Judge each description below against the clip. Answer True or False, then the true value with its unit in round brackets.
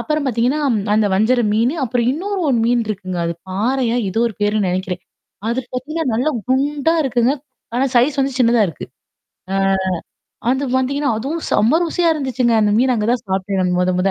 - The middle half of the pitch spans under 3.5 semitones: False (4.3 semitones)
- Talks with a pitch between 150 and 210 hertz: False (245 Hz)